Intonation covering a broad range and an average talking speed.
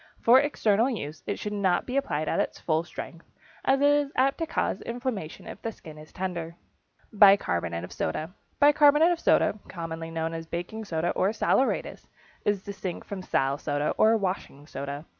Yes: wide, 6.6 semitones; average, 175 wpm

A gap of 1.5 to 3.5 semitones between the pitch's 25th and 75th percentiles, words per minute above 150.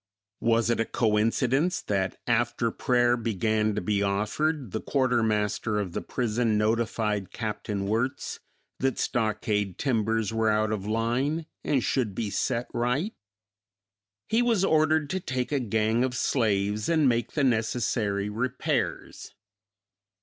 No: average, 3.2 semitones; slow, 135 wpm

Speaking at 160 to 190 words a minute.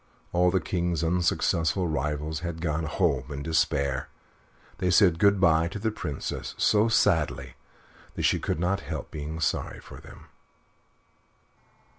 No: average, 140 wpm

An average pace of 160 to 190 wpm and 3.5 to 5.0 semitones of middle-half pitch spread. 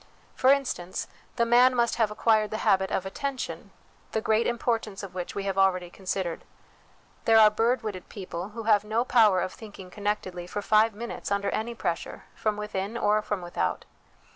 No: average, 180 wpm; average, 2.9 semitones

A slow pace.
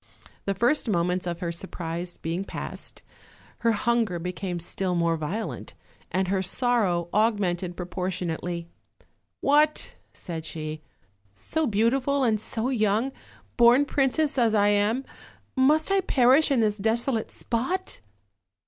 Yes: slow, 130 wpm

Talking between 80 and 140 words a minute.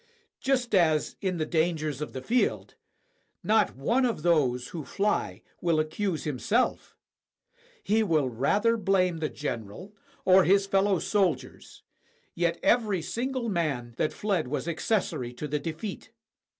Yes: slow, 135 wpm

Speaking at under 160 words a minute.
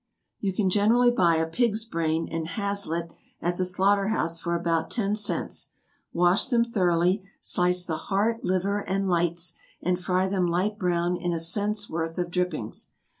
No: average, 175 wpm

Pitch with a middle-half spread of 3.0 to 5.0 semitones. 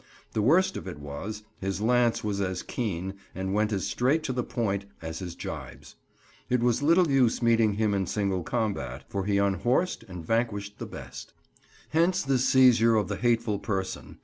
Yes: average, 4.1 semitones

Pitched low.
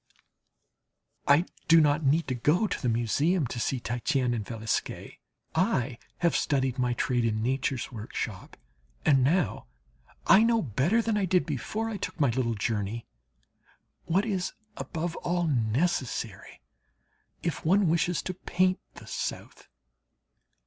No: medium, 145 Hz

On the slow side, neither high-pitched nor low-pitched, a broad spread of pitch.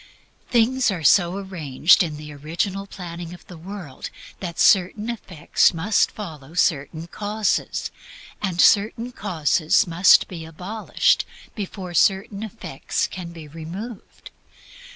No: slow, 120 wpm; medium, 180 Hz; average, 3.9 semitones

